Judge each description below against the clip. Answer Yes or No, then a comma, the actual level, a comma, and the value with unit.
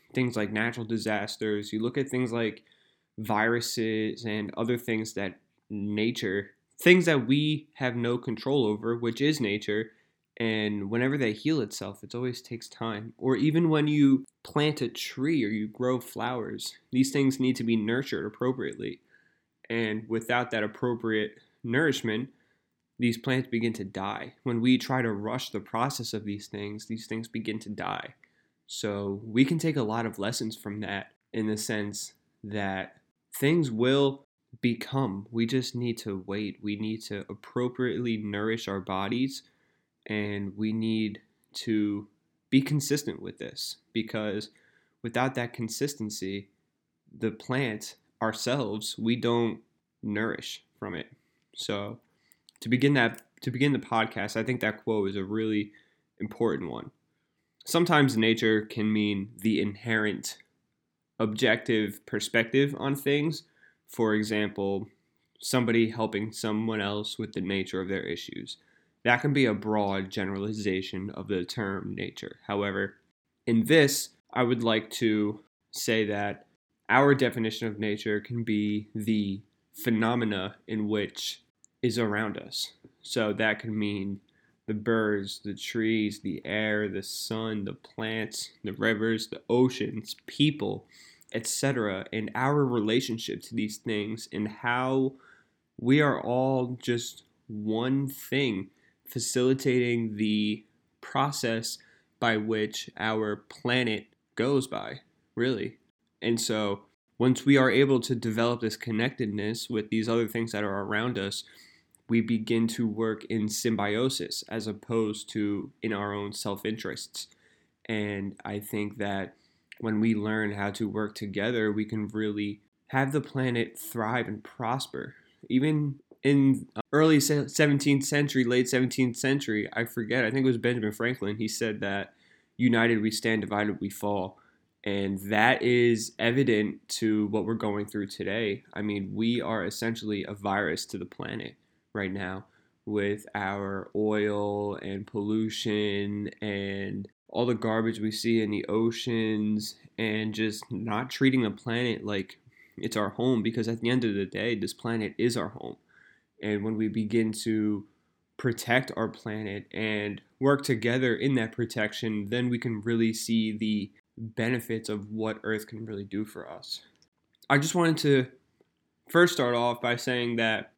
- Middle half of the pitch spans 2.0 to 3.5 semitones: Yes, average, 2.7 semitones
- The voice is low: Yes, low, 110 Hz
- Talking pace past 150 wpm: No, average, 145 wpm